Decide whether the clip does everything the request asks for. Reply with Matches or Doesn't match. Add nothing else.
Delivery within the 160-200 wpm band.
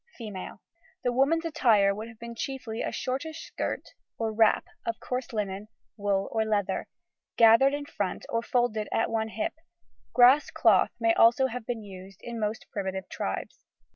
Matches